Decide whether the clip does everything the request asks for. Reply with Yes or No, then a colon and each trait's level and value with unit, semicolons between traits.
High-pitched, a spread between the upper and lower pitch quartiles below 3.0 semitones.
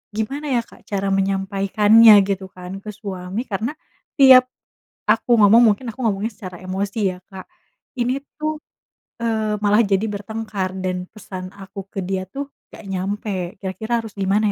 Yes: high, 205 Hz; narrow, 2.6 semitones